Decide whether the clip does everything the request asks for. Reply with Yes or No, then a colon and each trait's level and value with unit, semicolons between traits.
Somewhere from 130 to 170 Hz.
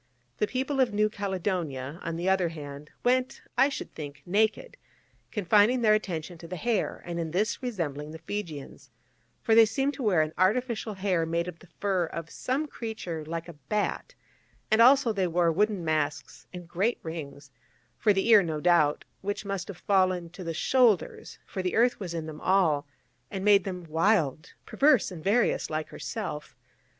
No: medium, 185 Hz